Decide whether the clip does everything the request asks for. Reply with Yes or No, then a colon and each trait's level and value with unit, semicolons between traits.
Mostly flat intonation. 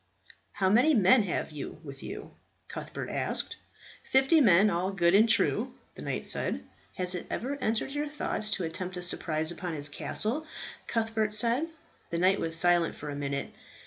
No: average, 5.1 semitones